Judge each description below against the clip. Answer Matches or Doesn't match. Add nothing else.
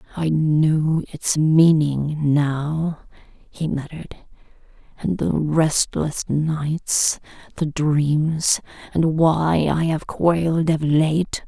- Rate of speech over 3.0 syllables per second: Doesn't match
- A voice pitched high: Doesn't match